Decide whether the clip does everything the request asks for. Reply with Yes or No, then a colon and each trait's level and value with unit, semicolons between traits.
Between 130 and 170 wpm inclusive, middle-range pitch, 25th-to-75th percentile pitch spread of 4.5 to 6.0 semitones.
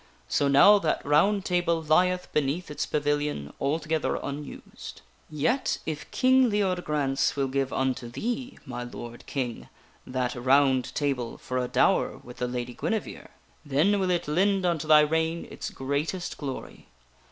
Yes: average, 145 wpm; medium, 150 Hz; average, 5.0 semitones